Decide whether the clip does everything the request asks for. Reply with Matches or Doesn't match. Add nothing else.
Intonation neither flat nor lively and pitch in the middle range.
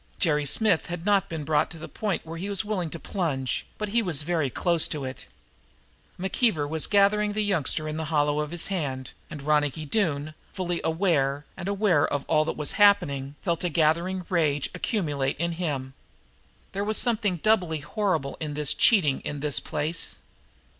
Matches